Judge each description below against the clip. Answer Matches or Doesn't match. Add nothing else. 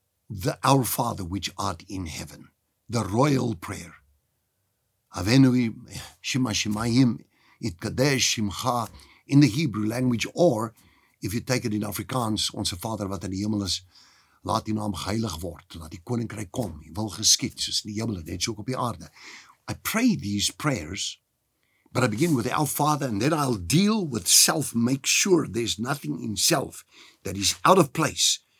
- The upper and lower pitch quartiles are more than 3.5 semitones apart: Matches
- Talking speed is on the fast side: Doesn't match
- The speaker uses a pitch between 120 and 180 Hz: Doesn't match